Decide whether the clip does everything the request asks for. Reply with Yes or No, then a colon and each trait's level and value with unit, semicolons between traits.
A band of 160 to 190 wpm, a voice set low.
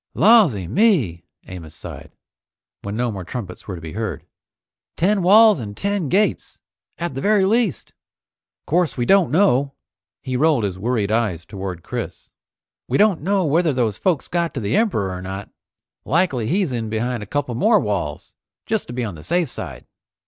Yes: average, 180 wpm; low, 125 Hz